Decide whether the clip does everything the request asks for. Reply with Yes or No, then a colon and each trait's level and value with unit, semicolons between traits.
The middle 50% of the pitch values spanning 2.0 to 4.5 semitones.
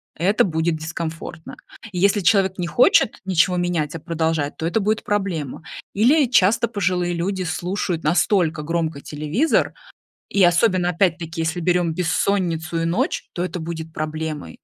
Yes: average, 2.8 semitones